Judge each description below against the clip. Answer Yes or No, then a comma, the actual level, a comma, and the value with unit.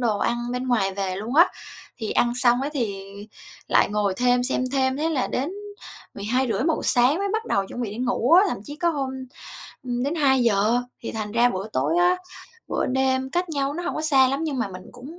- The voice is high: Yes, very high, 255 Hz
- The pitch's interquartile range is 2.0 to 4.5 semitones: Yes, average, 4.2 semitones